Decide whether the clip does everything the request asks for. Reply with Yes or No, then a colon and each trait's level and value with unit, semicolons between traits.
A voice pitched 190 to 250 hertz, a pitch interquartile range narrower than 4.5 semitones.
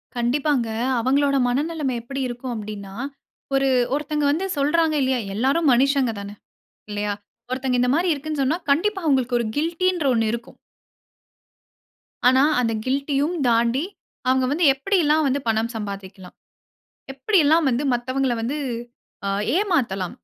No: very high, 270 Hz; average, 4.0 semitones